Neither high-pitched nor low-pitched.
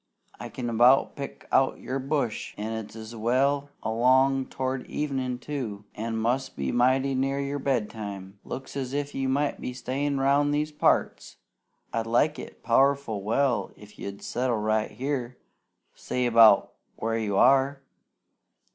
No: low, 130 Hz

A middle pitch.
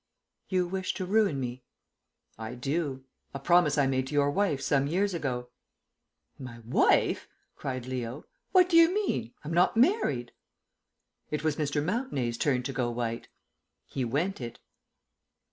Yes: medium, 145 Hz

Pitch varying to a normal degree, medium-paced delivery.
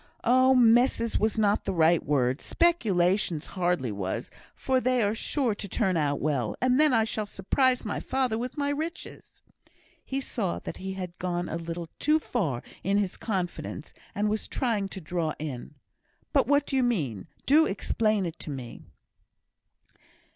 No: wide, 6.9 semitones; average, 170 wpm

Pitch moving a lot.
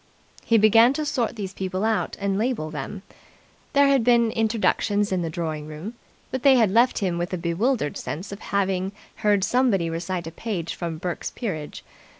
No: average, 5.0 semitones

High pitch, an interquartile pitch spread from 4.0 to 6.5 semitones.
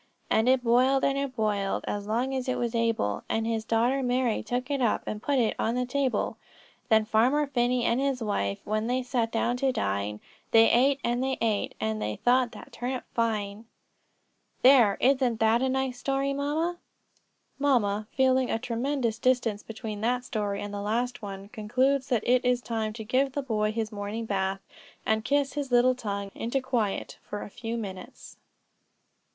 No: high, 235 Hz; average, 3.2 semitones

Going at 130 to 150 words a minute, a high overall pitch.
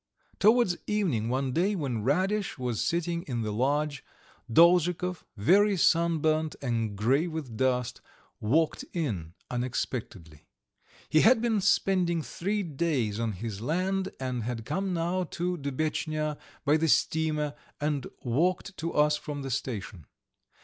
No: slow, 135 wpm; medium, 150 Hz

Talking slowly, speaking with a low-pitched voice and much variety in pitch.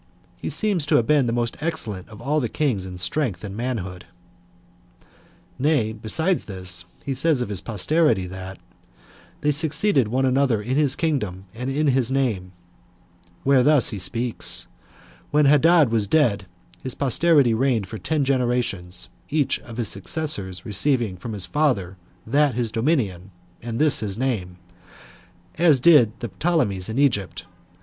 No: average, 155 wpm; low, 125 Hz; wide, 6.3 semitones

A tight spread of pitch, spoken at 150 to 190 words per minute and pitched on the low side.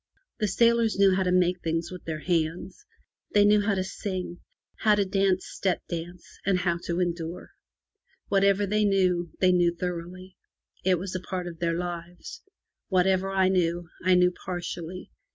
No: narrow, 1.8 semitones; average, 170 wpm; medium, 180 Hz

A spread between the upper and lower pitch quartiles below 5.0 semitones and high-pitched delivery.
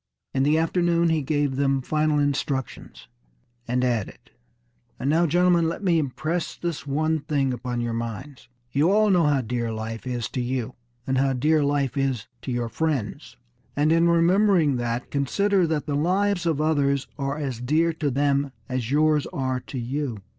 No: average, 4.0 semitones; medium, 140 Hz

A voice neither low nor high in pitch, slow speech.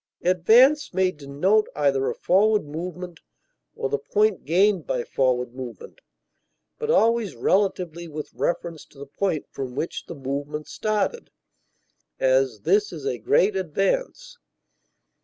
Yes: medium, 170 Hz; slow, 130 wpm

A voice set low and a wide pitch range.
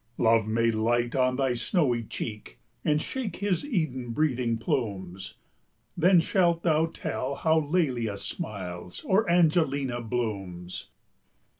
Yes: low, 125 Hz; wide, 6.3 semitones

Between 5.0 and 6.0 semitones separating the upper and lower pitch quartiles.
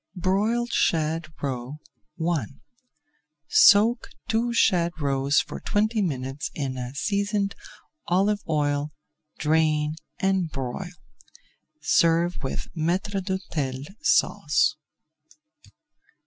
Yes: average, 5.3 semitones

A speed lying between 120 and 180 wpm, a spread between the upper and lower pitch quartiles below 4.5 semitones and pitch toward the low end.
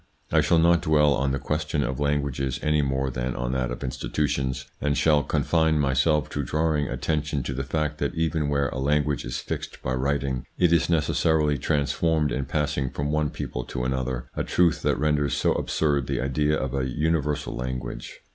No: average, 190 wpm; average, 2.7 semitones; very low, 70 Hz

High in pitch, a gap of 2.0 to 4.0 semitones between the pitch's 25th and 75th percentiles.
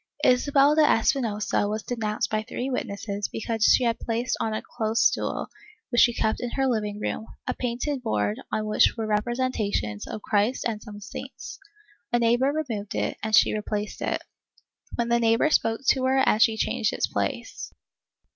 Yes: high, 225 Hz; average, 2.7 semitones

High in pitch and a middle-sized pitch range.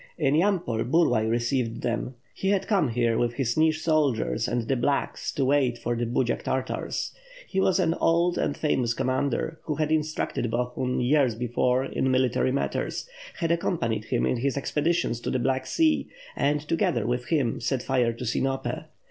No: low, 130 Hz; average, 4.5 semitones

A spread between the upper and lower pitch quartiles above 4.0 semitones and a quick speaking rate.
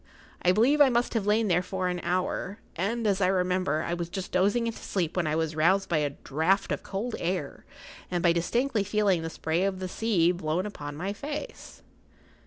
No: average, 3.5 semitones; fast, 210 wpm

